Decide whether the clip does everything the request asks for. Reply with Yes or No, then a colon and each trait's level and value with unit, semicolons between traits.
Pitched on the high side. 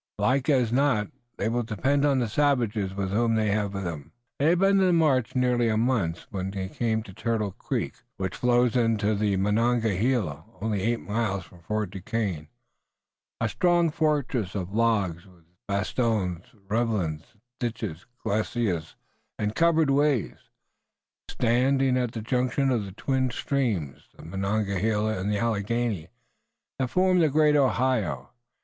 No: low, 115 Hz